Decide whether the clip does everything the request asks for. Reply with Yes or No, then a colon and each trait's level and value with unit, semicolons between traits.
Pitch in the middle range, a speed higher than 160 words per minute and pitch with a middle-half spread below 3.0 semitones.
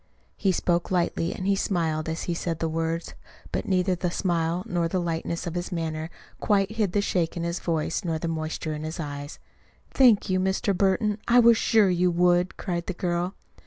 Yes: medium, 175 Hz; average, 200 wpm; narrow, 2.4 semitones